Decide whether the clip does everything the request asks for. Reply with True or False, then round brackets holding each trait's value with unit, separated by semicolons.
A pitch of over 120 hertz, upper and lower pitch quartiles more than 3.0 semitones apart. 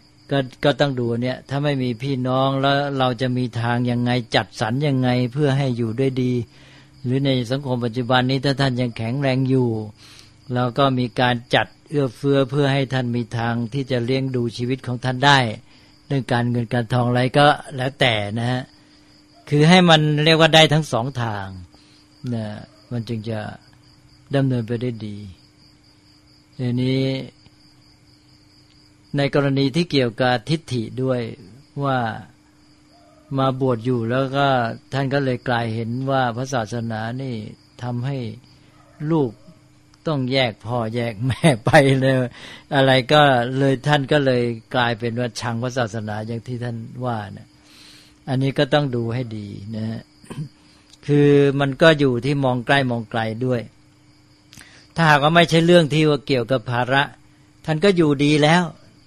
False (130 Hz; 2.7 semitones)